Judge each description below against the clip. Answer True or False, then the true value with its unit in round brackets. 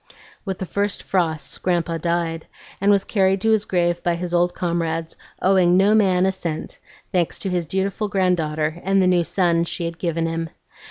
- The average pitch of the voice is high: False (175 Hz)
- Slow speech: False (185 wpm)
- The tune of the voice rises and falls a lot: False (2.4 semitones)